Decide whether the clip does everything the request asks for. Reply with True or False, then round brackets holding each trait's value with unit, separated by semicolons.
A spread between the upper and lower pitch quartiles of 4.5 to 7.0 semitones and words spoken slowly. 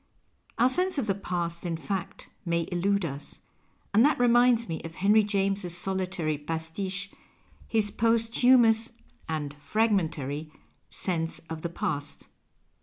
True (5.4 semitones; 130 wpm)